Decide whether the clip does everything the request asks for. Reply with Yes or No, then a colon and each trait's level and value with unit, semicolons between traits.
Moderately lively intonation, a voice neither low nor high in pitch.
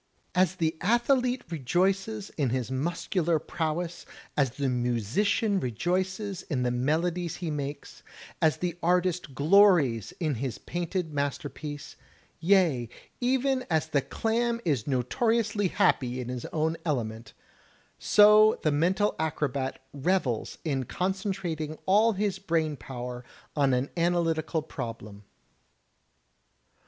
No: wide, 6.0 semitones; medium, 160 Hz